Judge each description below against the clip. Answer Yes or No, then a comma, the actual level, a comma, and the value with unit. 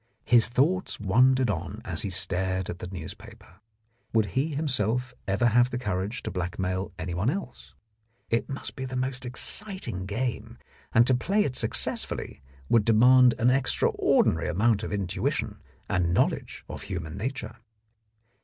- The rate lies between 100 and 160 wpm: Yes, average, 145 wpm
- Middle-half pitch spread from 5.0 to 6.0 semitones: Yes, wide, 5.5 semitones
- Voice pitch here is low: Yes, low, 115 Hz